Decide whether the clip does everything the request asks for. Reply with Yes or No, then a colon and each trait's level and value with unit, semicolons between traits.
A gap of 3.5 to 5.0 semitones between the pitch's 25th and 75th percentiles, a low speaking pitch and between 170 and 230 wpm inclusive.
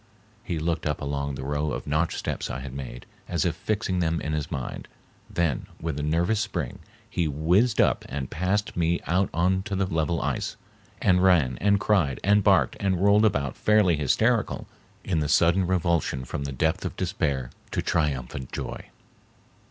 Yes: average, 4.5 semitones; very low, 85 Hz; average, 180 wpm